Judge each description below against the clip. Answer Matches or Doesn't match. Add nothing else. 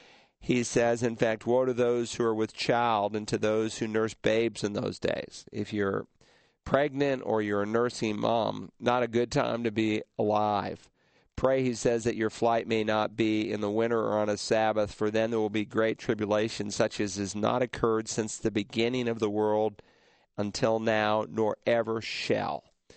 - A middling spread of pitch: Doesn't match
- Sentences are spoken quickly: Doesn't match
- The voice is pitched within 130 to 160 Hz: Doesn't match